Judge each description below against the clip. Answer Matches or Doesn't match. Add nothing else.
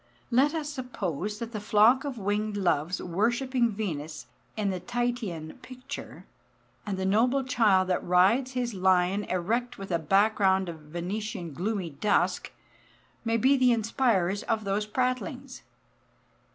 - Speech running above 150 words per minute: Doesn't match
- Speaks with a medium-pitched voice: Doesn't match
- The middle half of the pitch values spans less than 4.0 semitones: Doesn't match